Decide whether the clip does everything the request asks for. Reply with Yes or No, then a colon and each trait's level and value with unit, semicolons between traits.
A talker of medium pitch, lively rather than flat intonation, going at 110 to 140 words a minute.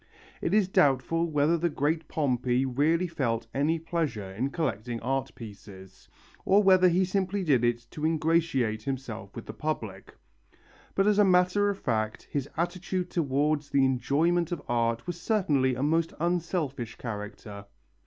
No: medium, 145 Hz; wide, 6.1 semitones; average, 155 wpm